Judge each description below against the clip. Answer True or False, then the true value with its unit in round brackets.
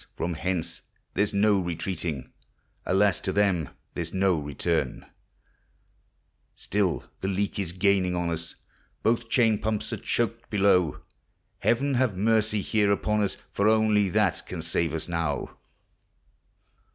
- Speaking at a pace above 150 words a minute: False (140 wpm)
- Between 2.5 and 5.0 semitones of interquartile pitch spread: True (3.7 semitones)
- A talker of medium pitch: False (95 Hz)